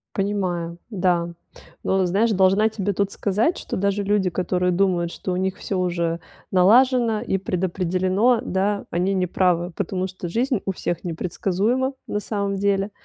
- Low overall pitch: No, high, 190 Hz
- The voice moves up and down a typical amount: No, narrow, 2.3 semitones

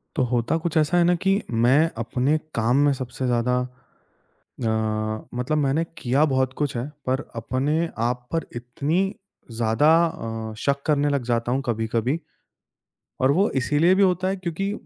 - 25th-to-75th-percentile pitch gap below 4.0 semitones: No, average, 4.7 semitones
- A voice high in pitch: No, low, 130 Hz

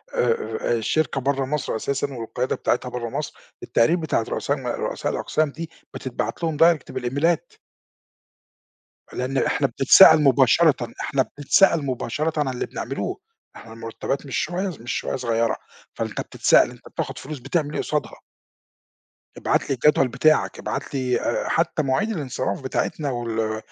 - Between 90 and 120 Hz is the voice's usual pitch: No, low, 135 Hz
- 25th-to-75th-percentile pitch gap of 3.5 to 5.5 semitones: Yes, average, 4.1 semitones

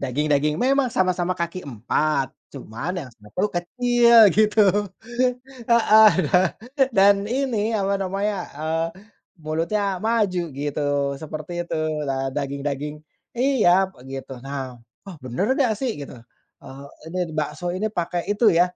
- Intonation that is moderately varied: No, wide, 6.6 semitones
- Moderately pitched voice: Yes, medium, 175 Hz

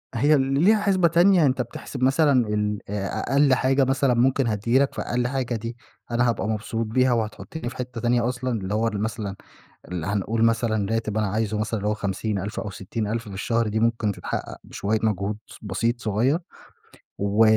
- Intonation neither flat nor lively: Yes, average, 3.4 semitones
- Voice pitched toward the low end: Yes, low, 115 Hz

